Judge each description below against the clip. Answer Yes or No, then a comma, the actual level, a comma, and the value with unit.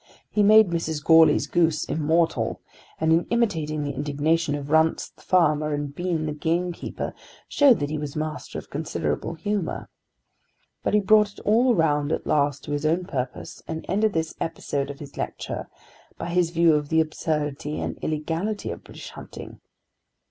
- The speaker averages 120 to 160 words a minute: No, average, 170 wpm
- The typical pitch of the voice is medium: Yes, medium, 160 Hz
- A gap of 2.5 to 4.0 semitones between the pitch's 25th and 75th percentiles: Yes, average, 2.9 semitones